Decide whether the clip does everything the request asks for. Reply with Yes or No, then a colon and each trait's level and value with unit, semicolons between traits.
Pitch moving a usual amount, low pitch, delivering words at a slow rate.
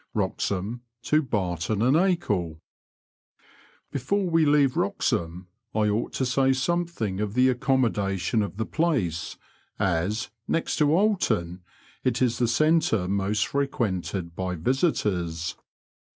No: wide, 7.3 semitones; low, 115 Hz; slow, 120 wpm